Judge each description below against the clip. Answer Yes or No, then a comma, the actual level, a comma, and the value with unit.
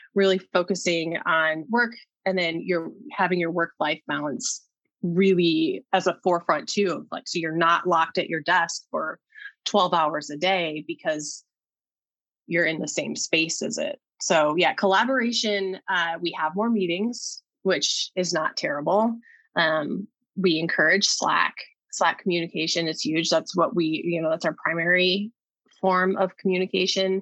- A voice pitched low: No, medium, 185 Hz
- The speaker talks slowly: No, average, 150 wpm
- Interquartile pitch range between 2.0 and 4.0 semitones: Yes, average, 3.4 semitones